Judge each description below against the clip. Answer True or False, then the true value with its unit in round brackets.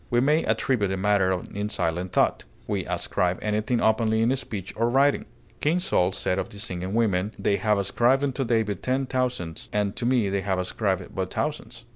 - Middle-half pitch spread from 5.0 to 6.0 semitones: False (4.4 semitones)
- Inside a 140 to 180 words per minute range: False (190 wpm)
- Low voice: True (105 Hz)